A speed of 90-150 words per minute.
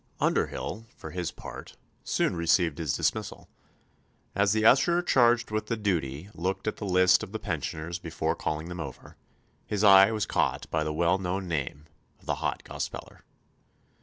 No: average, 165 wpm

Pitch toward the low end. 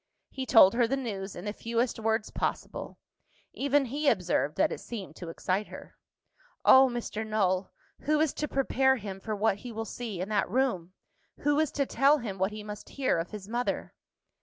No: high, 225 Hz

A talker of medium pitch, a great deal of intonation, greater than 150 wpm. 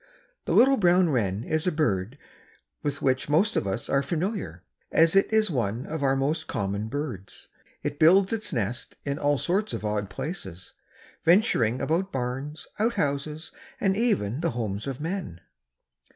Yes: medium, 145 Hz; wide, 7.4 semitones; average, 160 wpm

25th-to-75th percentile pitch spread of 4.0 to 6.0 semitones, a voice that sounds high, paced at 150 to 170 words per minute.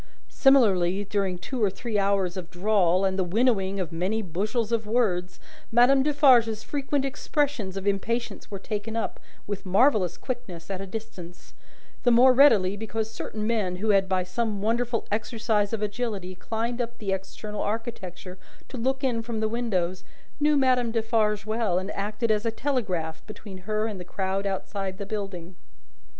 No: average, 3.5 semitones; high, 210 Hz; average, 165 wpm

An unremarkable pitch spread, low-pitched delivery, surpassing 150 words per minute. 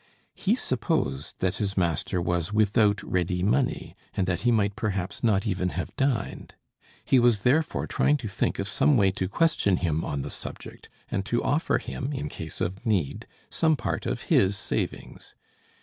Yes: average, 4.7 semitones; low, 100 Hz; average, 175 wpm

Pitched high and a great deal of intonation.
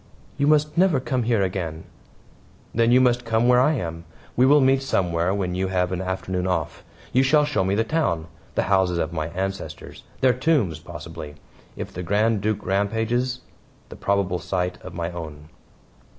No: low, 100 Hz; wide, 5.9 semitones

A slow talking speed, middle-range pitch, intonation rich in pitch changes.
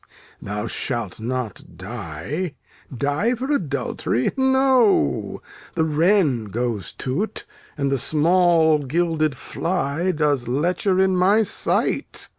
Yes: slow, 105 wpm; medium, 150 Hz; wide, 6.9 semitones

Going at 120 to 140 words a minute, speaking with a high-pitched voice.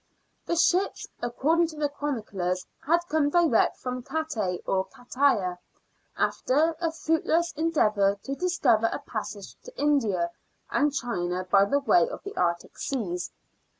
Yes: slow, 135 wpm; very high, 270 Hz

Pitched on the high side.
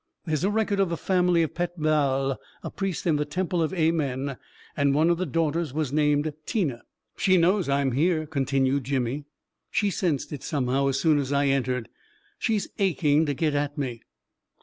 No: medium, 150 Hz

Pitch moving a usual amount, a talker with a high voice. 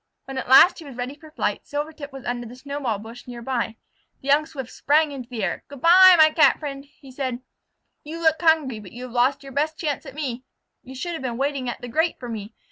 Yes: average, 3.8 semitones; very high, 270 Hz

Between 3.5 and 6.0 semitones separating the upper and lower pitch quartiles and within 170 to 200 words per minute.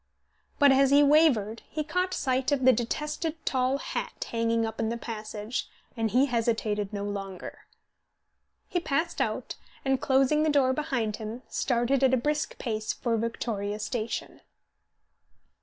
No: average, 4.1 semitones; average, 150 wpm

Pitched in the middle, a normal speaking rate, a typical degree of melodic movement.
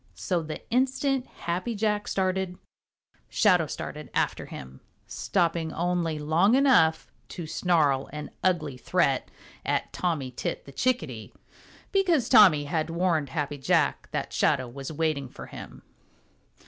No: medium, 165 Hz; slow, 130 wpm; average, 4.4 semitones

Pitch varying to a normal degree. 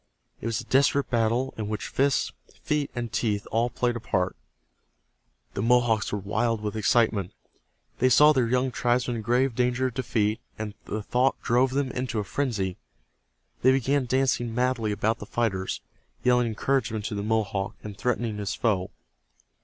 Yes: average, 3.1 semitones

